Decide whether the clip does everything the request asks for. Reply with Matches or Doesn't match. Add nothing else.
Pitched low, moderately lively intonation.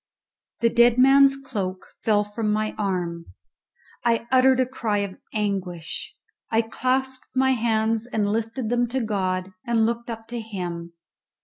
Doesn't match